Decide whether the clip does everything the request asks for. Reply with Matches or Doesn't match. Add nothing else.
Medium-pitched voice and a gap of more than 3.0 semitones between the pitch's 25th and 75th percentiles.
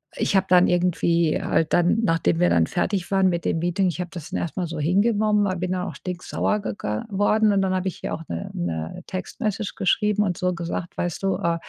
Doesn't match